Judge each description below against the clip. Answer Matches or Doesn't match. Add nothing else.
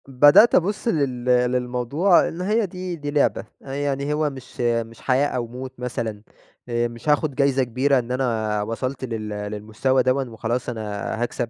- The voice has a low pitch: Matches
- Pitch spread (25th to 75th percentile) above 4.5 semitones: Doesn't match